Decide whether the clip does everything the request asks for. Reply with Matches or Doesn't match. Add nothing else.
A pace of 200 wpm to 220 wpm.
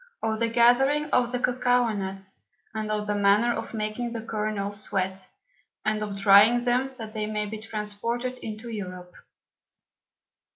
Doesn't match